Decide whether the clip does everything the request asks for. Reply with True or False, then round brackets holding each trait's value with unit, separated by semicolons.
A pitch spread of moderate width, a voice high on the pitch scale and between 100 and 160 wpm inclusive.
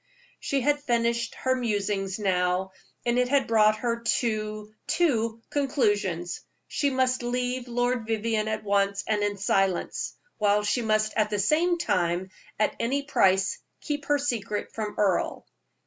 True (3.4 semitones; 220 Hz; 150 wpm)